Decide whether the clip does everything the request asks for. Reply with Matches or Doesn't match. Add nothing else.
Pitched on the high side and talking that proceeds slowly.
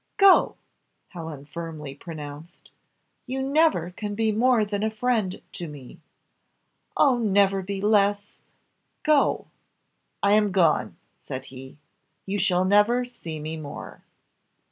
Matches